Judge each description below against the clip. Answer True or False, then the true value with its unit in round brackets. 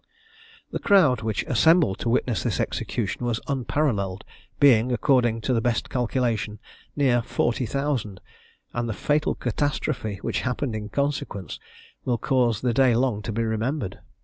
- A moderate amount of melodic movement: True (3.6 semitones)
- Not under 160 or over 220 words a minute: False (145 wpm)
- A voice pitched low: True (120 Hz)